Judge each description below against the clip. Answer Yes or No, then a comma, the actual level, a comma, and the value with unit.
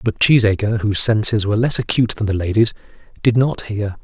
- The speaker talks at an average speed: Yes, average, 195 wpm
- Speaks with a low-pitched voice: Yes, low, 110 Hz